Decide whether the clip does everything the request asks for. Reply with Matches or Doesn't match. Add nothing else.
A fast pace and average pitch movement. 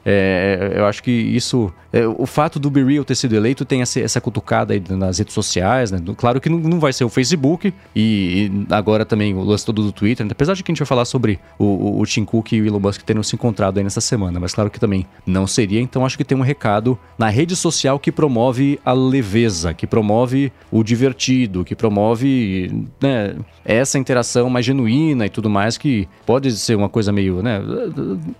Matches